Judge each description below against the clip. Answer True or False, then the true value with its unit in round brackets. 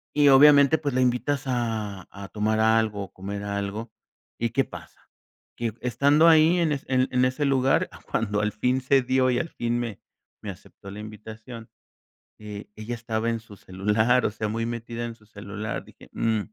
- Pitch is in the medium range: False (115 Hz)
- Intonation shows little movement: False (3.4 semitones)